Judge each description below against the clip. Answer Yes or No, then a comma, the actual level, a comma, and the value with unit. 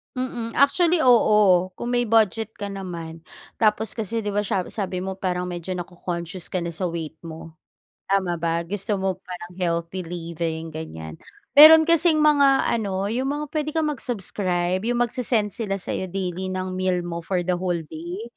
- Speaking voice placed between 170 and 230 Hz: Yes, high, 190 Hz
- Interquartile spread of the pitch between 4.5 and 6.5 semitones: Yes, average, 5.1 semitones